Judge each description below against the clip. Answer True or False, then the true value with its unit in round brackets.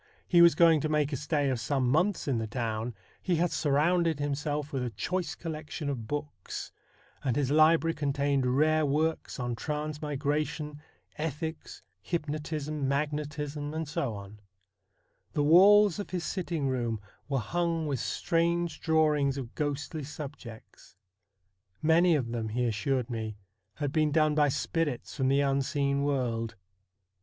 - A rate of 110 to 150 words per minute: True (140 wpm)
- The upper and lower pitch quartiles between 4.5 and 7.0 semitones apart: False (2.8 semitones)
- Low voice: False (145 Hz)